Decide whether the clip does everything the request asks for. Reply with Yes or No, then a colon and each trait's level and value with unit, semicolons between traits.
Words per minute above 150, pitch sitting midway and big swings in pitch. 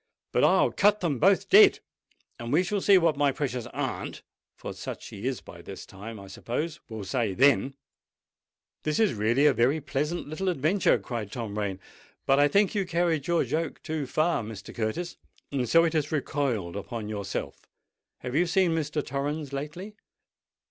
Yes: average, 170 wpm; medium, 145 Hz; wide, 6.1 semitones